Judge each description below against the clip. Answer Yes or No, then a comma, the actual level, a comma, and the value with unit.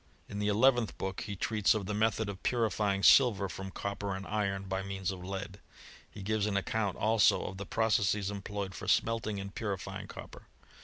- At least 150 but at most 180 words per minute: No, average, 190 wpm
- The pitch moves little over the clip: Yes, narrow, 1.8 semitones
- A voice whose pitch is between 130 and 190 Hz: No, low, 100 Hz